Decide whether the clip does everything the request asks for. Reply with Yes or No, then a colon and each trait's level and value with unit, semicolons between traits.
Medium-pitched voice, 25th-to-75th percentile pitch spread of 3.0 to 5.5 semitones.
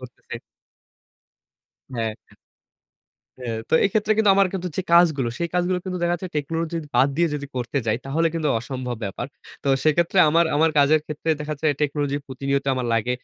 Yes: medium, 150 Hz; average, 4.4 semitones